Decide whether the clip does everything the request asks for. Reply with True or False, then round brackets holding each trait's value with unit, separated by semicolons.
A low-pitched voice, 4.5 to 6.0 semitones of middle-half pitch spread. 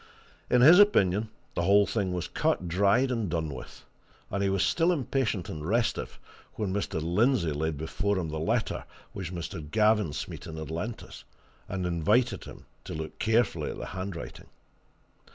True (95 Hz; 5.1 semitones)